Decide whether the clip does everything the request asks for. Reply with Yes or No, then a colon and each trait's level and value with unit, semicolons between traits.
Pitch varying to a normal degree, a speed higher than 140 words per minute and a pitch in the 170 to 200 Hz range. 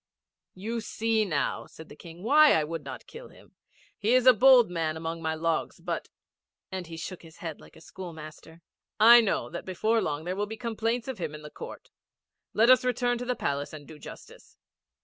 No: wide, 6.3 semitones; fast, 205 wpm; medium, 185 Hz